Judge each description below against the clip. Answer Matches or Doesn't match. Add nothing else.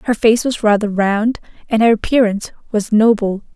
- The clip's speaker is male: Doesn't match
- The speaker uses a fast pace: Doesn't match